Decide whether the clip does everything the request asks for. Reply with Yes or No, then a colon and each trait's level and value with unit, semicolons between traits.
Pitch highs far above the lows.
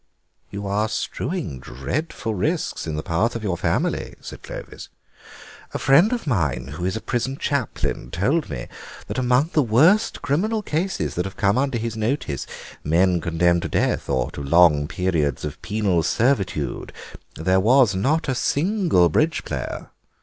Yes: wide, 8.6 semitones